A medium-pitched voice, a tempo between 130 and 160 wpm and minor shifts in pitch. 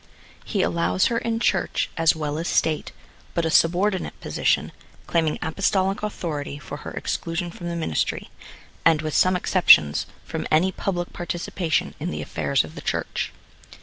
No: medium, 165 Hz; average, 155 wpm; average, 3.3 semitones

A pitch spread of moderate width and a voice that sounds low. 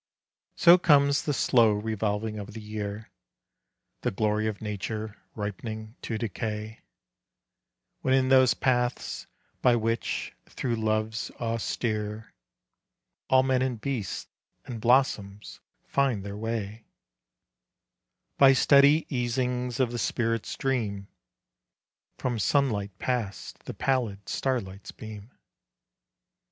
Yes: average, 3.2 semitones; low, 115 Hz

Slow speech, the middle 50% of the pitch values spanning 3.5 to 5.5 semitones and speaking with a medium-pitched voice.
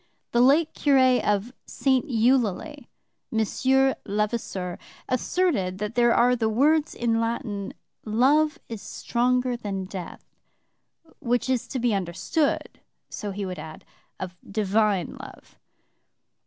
No: slow, 120 wpm; average, 4.1 semitones; high, 235 Hz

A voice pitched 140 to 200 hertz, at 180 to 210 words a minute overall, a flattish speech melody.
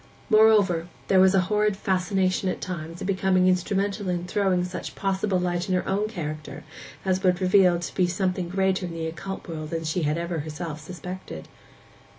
Yes: medium, 185 Hz; average, 185 wpm; narrow, 2.0 semitones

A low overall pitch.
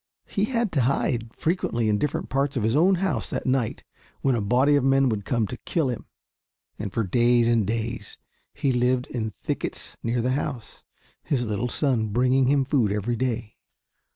Yes: low, 125 Hz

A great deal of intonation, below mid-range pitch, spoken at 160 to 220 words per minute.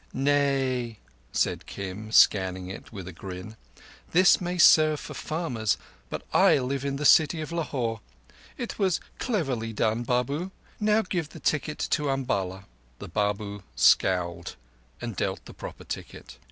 No: wide, 7.1 semitones; low, 125 Hz; average, 145 wpm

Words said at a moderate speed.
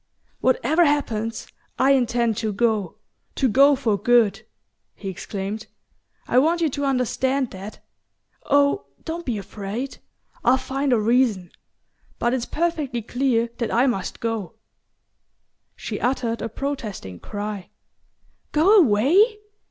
No: slow, 125 wpm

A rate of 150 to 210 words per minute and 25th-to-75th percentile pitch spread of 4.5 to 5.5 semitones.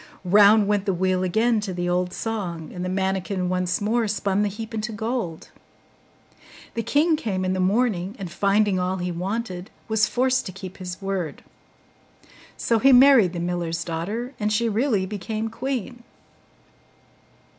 No: average, 160 wpm; average, 3.6 semitones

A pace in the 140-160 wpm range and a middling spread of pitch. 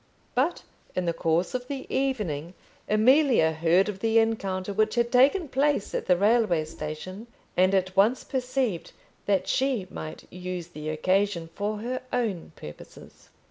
No: average, 150 wpm; wide, 6.0 semitones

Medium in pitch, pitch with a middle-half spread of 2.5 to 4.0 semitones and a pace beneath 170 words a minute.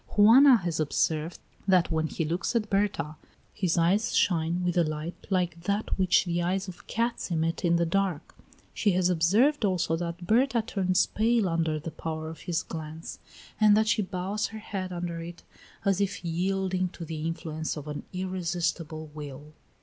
No: medium, 175 Hz; average, 3.2 semitones; average, 175 wpm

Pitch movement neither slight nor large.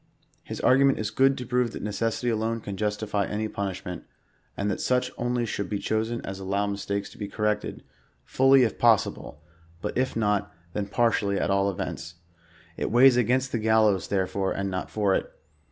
Yes: average, 3.1 semitones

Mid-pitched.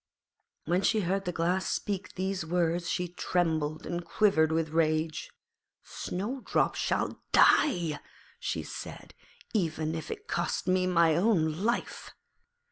Yes: medium, 175 Hz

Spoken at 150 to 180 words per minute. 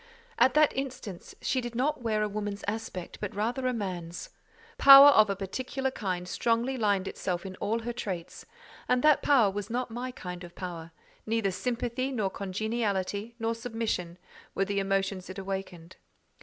Yes: average, 170 wpm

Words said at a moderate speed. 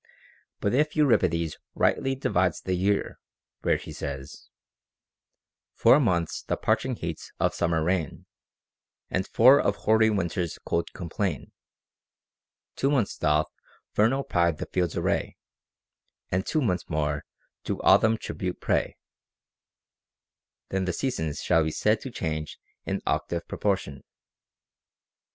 No: slow, 125 wpm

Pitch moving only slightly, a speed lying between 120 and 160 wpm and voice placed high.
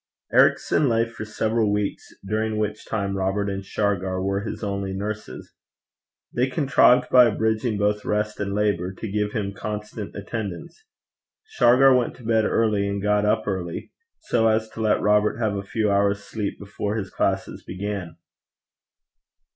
No: narrow, 1.8 semitones; average, 155 wpm; low, 105 Hz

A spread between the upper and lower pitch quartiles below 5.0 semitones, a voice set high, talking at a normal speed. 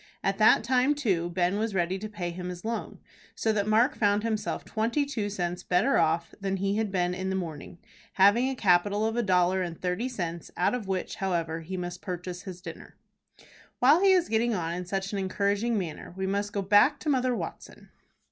No: average, 3.7 semitones; high, 195 Hz; fast, 210 wpm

